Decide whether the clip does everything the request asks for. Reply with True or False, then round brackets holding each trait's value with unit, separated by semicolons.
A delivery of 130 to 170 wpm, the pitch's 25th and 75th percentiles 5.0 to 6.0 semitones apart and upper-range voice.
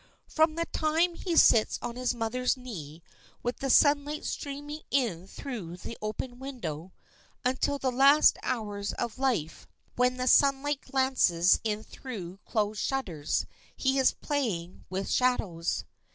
True (135 wpm; 5.4 semitones; 250 Hz)